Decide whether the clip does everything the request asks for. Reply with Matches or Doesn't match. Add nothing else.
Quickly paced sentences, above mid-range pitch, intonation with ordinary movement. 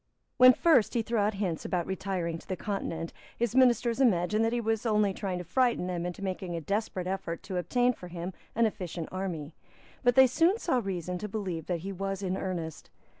Matches